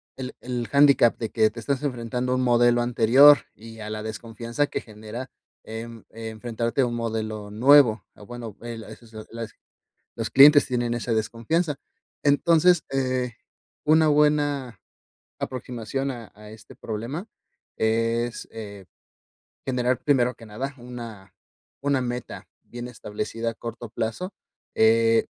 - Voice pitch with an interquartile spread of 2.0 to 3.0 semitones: Yes, average, 2.7 semitones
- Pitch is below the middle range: Yes, low, 120 Hz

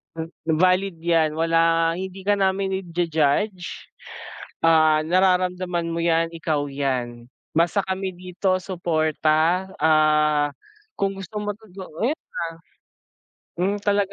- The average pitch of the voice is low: No, medium, 170 Hz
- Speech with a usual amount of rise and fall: Yes, average, 3.2 semitones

